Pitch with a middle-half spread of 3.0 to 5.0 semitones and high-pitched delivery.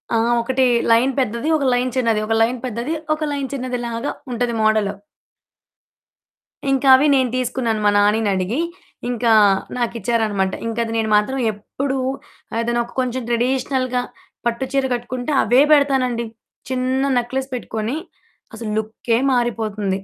No: narrow, 2.5 semitones; high, 240 Hz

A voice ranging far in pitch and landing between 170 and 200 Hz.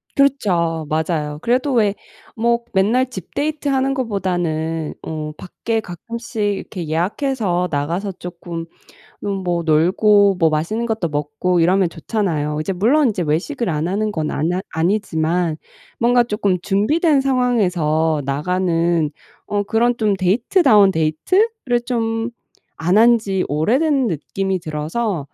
Yes: wide, 6.0 semitones; high, 190 Hz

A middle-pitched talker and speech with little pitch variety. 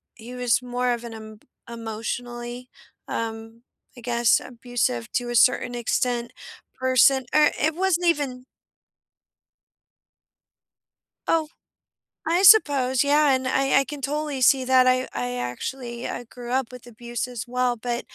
No: very high, 250 Hz; narrow, 2.0 semitones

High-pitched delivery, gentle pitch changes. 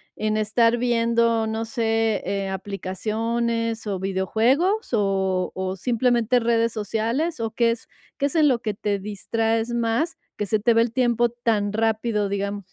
Yes: high, 225 Hz; narrow, 2.3 semitones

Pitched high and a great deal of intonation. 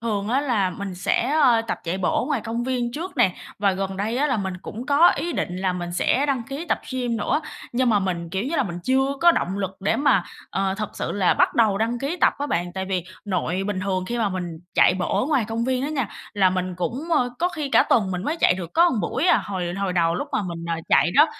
Yes: high, 210 Hz; wide, 5.9 semitones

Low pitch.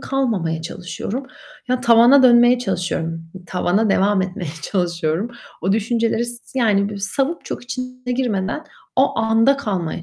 No: high, 220 Hz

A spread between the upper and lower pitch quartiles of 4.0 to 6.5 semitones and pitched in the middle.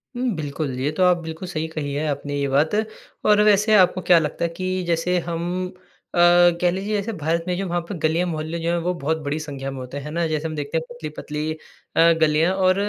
No: average, 3.2 semitones; medium, 165 Hz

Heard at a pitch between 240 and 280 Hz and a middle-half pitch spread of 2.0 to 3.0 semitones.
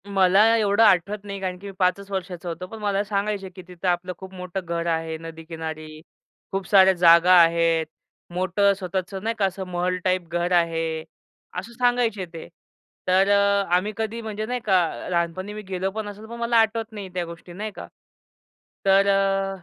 No: high, 190 Hz; narrow, 2.6 semitones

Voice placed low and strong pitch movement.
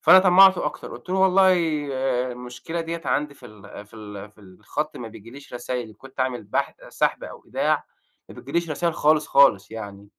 Yes: low, 130 Hz; wide, 7.7 semitones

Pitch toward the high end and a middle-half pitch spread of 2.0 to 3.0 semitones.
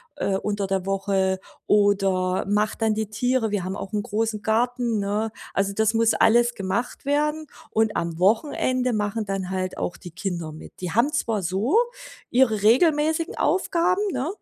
No: high, 215 Hz; average, 4.0 semitones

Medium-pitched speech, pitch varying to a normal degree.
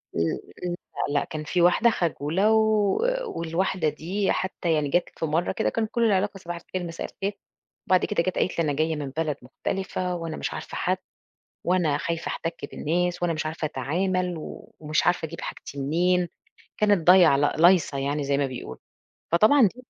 Yes: medium, 170 Hz; average, 3.3 semitones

